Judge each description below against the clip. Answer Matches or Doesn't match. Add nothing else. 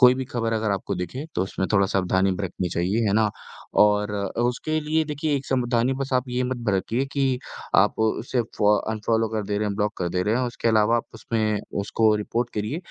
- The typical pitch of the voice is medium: Doesn't match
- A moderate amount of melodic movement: Matches